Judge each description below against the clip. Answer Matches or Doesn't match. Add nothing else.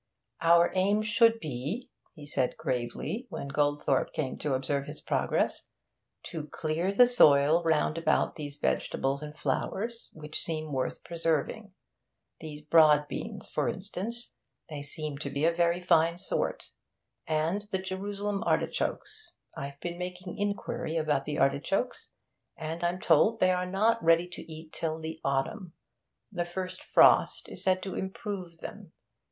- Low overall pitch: Doesn't match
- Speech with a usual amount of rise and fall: Matches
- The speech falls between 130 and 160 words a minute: Matches